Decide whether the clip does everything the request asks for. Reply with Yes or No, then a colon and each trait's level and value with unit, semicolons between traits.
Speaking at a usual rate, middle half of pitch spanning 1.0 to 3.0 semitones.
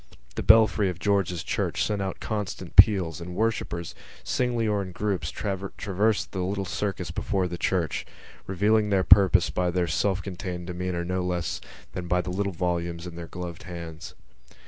Yes: average, 170 wpm; narrow, 2.4 semitones